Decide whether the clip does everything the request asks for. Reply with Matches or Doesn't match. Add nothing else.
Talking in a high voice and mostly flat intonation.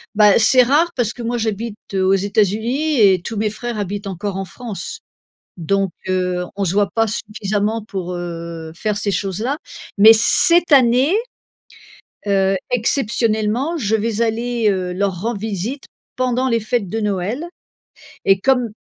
Doesn't match